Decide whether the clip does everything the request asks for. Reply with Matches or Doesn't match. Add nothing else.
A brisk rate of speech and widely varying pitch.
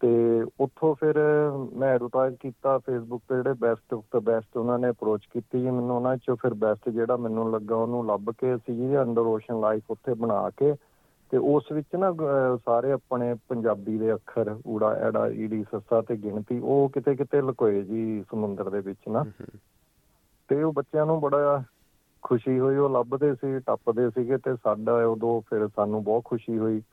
Doesn't match